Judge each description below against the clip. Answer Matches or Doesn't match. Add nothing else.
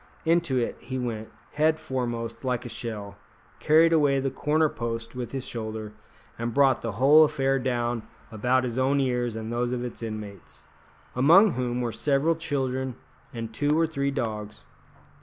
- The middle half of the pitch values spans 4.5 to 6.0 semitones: Doesn't match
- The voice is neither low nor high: Doesn't match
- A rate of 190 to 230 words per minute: Doesn't match